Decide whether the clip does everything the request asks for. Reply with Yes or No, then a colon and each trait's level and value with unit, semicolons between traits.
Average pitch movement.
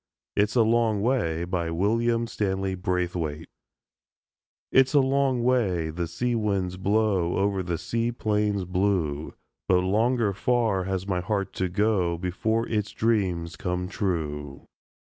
Yes: average, 4.0 semitones